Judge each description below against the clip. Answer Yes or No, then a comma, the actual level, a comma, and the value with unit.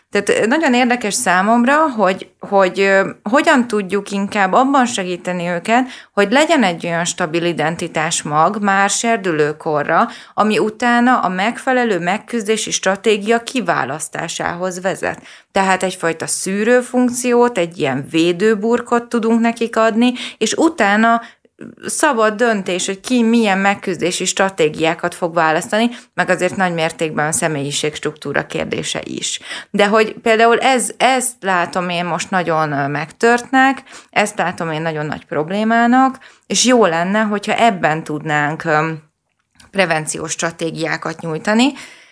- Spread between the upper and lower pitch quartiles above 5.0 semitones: Yes, wide, 5.4 semitones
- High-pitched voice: Yes, high, 200 Hz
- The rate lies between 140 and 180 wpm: No, average, 120 wpm